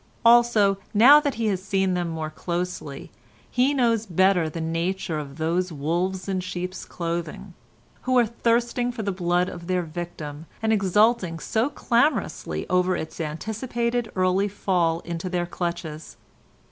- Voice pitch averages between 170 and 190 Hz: Yes, medium, 185 Hz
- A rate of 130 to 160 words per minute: Yes, average, 145 wpm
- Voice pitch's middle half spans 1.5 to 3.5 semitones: No, average, 4.6 semitones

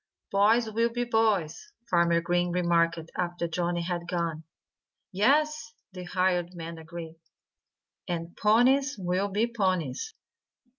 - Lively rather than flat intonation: No, average, 4.5 semitones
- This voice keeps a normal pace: No, slow, 115 wpm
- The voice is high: No, medium, 180 Hz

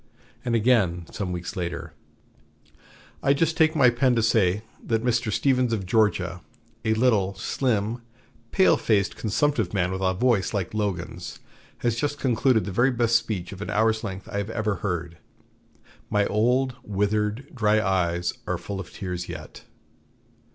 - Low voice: Yes, low, 110 Hz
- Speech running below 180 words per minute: Yes, average, 155 wpm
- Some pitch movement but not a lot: Yes, average, 4.2 semitones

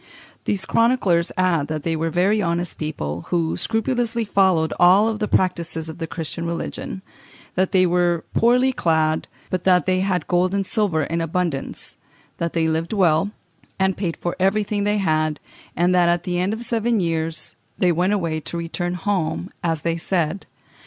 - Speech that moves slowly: No, average, 175 wpm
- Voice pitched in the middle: Yes, medium, 175 Hz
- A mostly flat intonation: No, average, 3.1 semitones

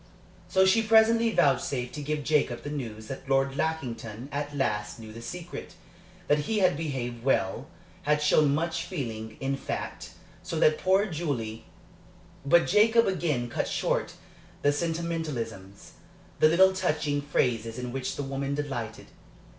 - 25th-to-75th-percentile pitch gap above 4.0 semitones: Yes, wide, 5.4 semitones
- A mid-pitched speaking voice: Yes, medium, 145 Hz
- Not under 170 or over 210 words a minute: No, average, 145 wpm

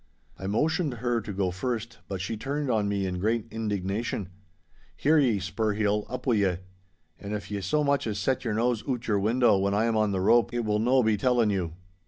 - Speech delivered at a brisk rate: Yes, fast, 225 wpm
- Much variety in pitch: No, average, 3.3 semitones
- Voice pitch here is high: No, low, 110 Hz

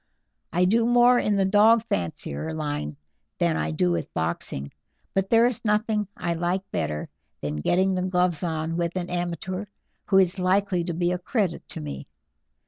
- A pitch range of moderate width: Yes, average, 4.7 semitones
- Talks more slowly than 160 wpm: No, average, 175 wpm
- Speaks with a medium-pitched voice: Yes, medium, 180 Hz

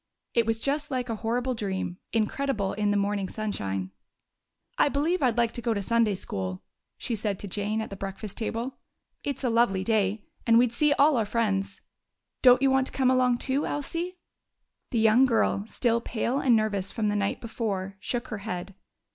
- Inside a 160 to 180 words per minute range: No, average, 190 wpm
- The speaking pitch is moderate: No, high, 225 Hz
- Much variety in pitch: No, average, 3.8 semitones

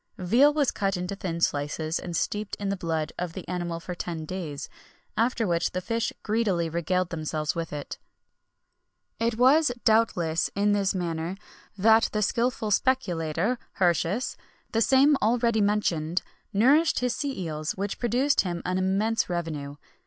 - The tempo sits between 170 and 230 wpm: No, average, 155 wpm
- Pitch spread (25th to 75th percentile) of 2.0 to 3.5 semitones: No, average, 5.3 semitones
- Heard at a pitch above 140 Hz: Yes, high, 190 Hz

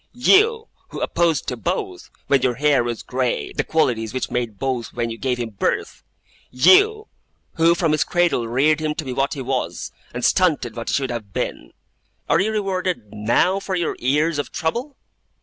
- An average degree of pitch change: No, wide, 6.0 semitones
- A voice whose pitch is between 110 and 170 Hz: Yes, medium, 140 Hz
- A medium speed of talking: Yes, average, 185 wpm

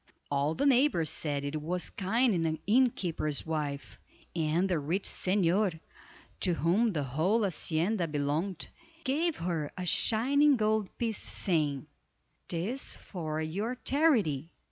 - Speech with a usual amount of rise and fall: No, wide, 5.9 semitones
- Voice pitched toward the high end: No, medium, 180 Hz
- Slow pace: Yes, slow, 130 wpm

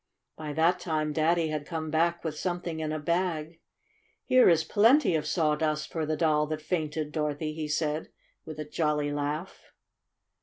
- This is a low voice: No, medium, 155 Hz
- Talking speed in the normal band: Yes, average, 165 wpm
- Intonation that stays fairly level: Yes, narrow, 1.9 semitones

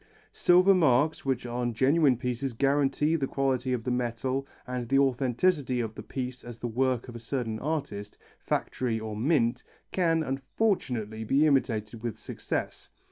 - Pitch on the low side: Yes, low, 130 Hz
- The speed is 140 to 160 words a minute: Yes, average, 155 wpm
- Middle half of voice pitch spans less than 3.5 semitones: Yes, average, 2.9 semitones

